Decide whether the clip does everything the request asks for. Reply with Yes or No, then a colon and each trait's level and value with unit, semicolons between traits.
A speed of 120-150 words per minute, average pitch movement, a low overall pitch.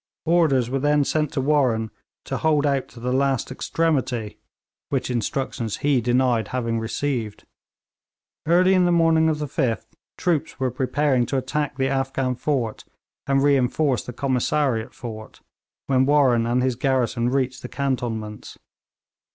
Yes: average, 145 wpm; average, 3.3 semitones; low, 130 Hz